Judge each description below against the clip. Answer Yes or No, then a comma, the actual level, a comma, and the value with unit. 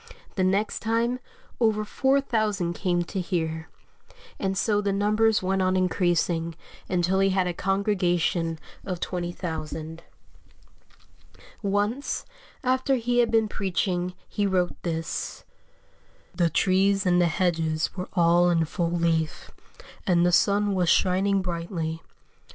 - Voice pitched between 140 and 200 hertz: Yes, medium, 185 Hz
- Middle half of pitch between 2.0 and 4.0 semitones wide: Yes, average, 2.9 semitones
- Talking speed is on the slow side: Yes, slow, 125 wpm